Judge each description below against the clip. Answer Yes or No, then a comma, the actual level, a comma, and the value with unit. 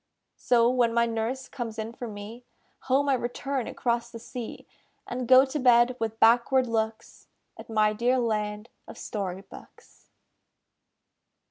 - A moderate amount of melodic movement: No, narrow, 2.2 semitones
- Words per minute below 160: Yes, average, 145 wpm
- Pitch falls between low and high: No, high, 235 Hz